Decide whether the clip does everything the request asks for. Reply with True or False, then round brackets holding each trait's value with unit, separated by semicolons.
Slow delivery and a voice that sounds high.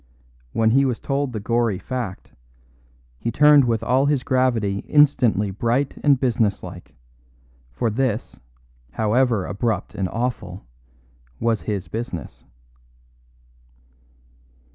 False (105 wpm; 115 Hz)